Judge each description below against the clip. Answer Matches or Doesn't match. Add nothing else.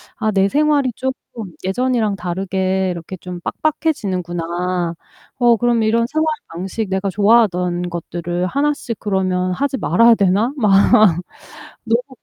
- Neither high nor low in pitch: Doesn't match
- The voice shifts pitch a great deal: Doesn't match